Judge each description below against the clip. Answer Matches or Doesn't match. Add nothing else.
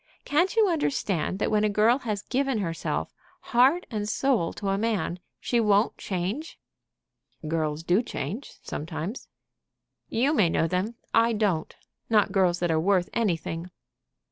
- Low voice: Doesn't match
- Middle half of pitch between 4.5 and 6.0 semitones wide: Matches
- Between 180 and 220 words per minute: Doesn't match